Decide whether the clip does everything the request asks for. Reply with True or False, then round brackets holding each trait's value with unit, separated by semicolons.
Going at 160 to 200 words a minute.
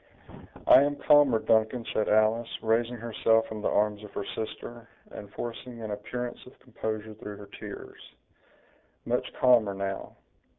False (145 wpm)